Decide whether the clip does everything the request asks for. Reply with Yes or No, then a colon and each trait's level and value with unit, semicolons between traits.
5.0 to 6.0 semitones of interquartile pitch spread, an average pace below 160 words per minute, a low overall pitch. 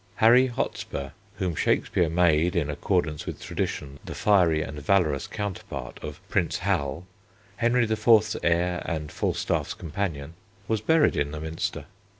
Yes: average, 5.3 semitones; average, 140 wpm; very low, 85 Hz